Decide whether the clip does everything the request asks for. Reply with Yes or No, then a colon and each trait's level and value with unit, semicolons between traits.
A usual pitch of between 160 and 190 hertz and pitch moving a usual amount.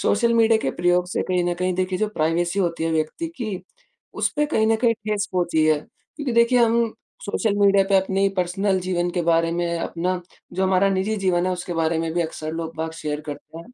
Yes: medium, 185 Hz; average, 3.7 semitones